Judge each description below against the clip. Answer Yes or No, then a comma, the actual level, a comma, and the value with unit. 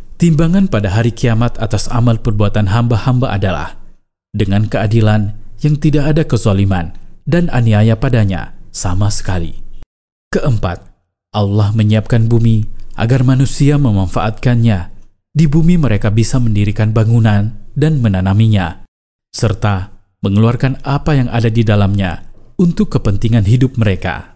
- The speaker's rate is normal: Yes, average, 115 wpm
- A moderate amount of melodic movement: Yes, average, 3.7 semitones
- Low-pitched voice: Yes, low, 110 Hz